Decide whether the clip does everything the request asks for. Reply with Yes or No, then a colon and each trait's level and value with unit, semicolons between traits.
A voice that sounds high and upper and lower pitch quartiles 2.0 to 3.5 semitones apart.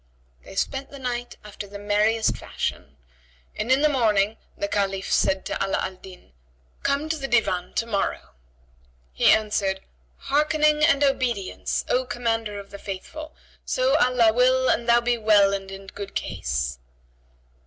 No: high, 220 Hz; average, 4.7 semitones